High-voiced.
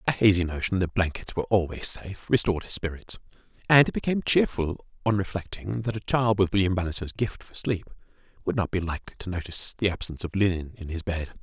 No: very low, 95 Hz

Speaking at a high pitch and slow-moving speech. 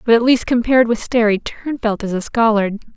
No: high, 225 Hz; fast, 205 wpm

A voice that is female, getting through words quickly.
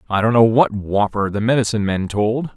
No: male; fast, 210 wpm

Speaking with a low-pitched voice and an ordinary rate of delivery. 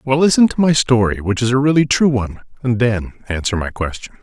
No: low, 125 Hz; fast, 225 wpm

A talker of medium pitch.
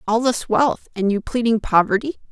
No: high, 225 Hz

